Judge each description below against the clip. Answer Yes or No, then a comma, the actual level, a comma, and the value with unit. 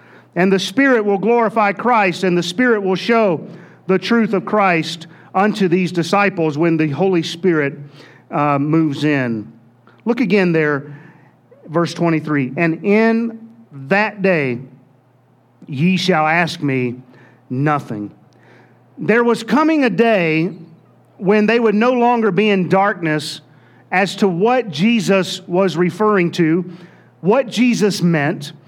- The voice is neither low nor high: Yes, medium, 175 Hz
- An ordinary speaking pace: No, slow, 130 wpm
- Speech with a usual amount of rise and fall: No, wide, 5.7 semitones